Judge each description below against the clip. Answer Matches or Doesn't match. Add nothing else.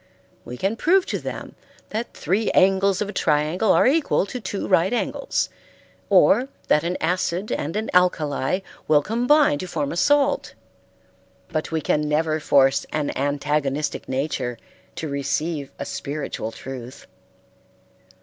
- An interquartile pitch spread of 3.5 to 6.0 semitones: Matches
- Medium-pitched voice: Matches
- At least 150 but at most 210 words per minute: Doesn't match